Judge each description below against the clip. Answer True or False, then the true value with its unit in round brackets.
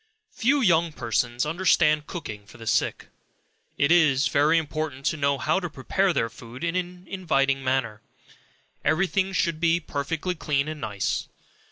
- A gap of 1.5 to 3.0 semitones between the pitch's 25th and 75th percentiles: False (4.4 semitones)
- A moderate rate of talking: True (160 wpm)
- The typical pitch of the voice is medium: True (155 Hz)